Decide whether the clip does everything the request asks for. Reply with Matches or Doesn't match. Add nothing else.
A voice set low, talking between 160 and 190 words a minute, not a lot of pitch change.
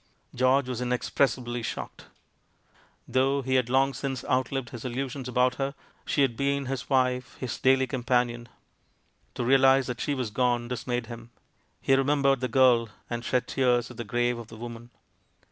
Matches